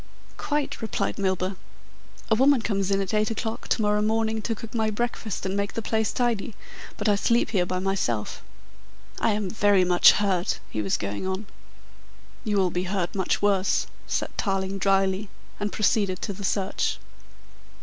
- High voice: Yes, high, 200 Hz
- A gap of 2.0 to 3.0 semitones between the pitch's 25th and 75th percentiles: Yes, narrow, 2.6 semitones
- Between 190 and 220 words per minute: No, average, 170 wpm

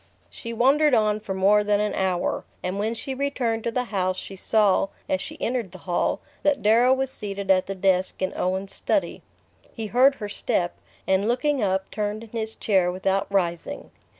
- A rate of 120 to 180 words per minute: No, average, 190 wpm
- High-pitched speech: Yes, high, 210 Hz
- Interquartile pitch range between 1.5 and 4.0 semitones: Yes, average, 3.6 semitones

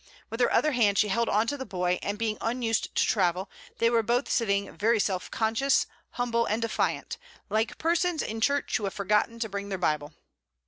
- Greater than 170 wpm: Yes, average, 200 wpm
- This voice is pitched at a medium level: No, high, 225 Hz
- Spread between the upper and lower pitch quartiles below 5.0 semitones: Yes, average, 2.8 semitones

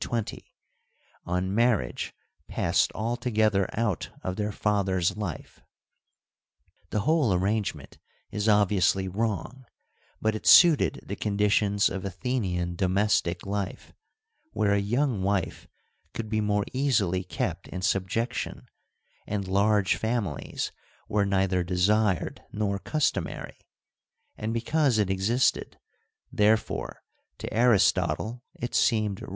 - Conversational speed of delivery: No, slow, 110 wpm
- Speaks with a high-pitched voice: No, low, 105 Hz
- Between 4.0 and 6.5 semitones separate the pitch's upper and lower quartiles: No, average, 2.8 semitones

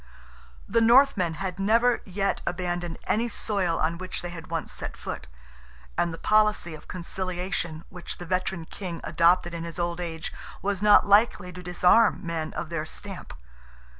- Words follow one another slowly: No, average, 165 wpm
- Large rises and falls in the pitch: No, average, 2.9 semitones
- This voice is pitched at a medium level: Yes, medium, 180 Hz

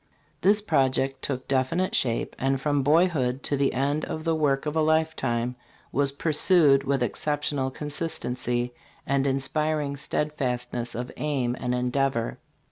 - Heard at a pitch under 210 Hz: Yes, medium, 140 Hz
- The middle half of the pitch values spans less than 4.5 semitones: Yes, average, 2.9 semitones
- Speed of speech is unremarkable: No, slow, 130 wpm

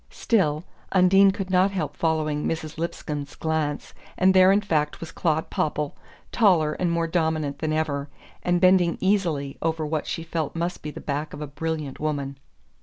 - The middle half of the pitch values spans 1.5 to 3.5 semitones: Yes, average, 3.2 semitones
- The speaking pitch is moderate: Yes, medium, 160 Hz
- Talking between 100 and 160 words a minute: No, average, 175 wpm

